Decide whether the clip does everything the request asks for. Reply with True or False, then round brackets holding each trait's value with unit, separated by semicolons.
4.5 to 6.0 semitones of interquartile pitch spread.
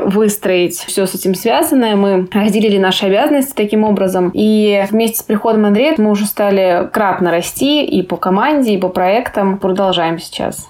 False (2.5 semitones)